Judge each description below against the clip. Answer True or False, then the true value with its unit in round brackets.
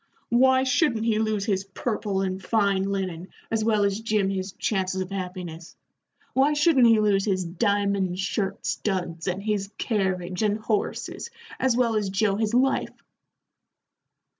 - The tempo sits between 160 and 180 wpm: False (150 wpm)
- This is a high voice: True (200 Hz)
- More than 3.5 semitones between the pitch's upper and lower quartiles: False (2.8 semitones)